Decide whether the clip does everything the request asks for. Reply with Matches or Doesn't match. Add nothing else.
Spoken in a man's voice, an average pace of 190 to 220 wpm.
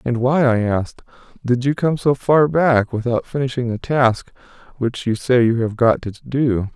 Matches